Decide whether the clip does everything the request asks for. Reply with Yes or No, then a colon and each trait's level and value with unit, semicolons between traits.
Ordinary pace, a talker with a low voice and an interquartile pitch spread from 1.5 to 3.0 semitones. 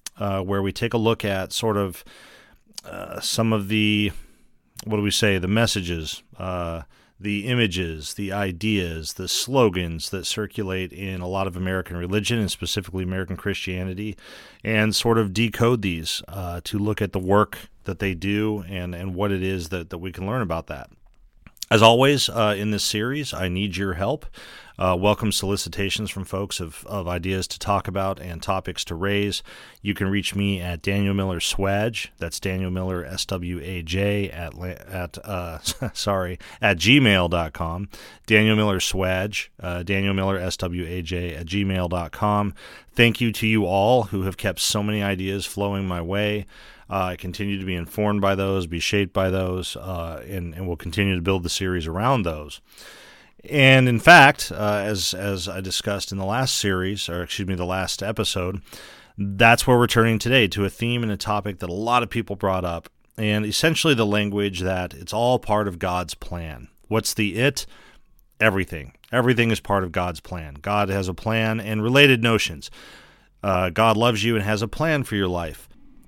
Yes: average, 180 wpm; low, 100 Hz; average, 2.7 semitones